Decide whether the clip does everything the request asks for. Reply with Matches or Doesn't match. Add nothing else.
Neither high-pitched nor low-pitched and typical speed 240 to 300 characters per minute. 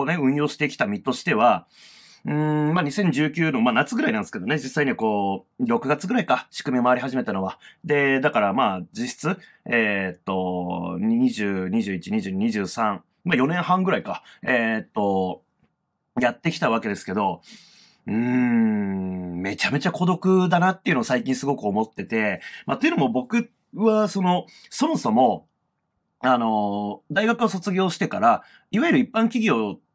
Matches